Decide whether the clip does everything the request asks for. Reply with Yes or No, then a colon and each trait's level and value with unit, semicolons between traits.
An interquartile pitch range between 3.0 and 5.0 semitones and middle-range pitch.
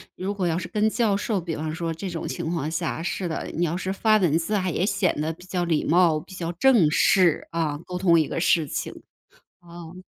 No: narrow, 2.5 semitones; medium, 175 Hz